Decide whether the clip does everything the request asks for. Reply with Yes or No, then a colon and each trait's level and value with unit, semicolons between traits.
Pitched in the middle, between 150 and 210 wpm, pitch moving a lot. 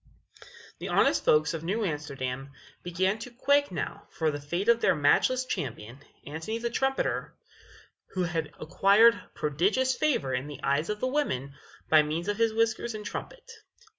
Yes: medium, 175 Hz; average, 165 wpm; wide, 7.6 semitones